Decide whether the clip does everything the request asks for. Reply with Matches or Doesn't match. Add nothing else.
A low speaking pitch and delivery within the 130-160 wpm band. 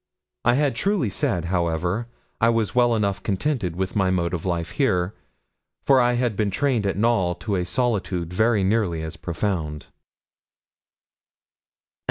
Matches